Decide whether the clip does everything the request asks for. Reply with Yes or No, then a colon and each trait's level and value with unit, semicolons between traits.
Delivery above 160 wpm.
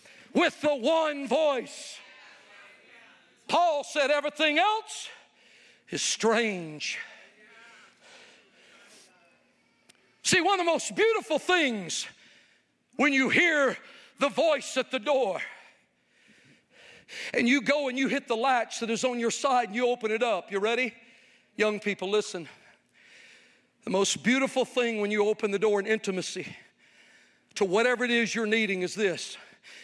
No: slow, 135 wpm